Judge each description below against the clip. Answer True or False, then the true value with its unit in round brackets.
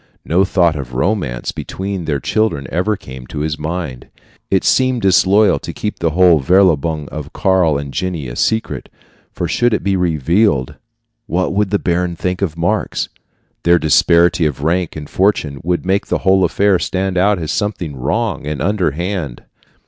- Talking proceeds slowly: False (170 wpm)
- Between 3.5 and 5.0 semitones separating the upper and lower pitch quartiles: True (4.2 semitones)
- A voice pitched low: True (90 Hz)